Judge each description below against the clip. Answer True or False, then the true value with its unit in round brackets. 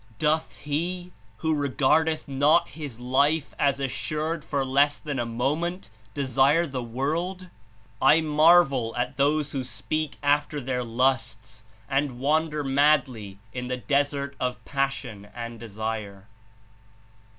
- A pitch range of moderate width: True (3.5 semitones)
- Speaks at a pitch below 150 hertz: True (140 Hz)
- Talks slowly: True (125 wpm)